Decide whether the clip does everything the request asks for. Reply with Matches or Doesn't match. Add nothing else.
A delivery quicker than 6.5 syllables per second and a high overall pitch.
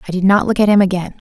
Matches